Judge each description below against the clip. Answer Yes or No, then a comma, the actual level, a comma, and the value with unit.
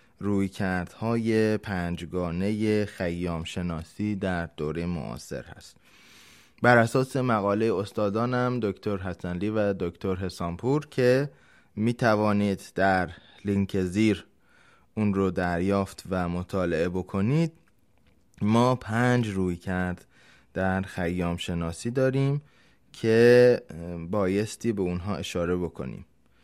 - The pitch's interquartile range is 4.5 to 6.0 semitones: No, average, 3.9 semitones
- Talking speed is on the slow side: Yes, slow, 100 wpm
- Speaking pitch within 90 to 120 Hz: Yes, low, 100 Hz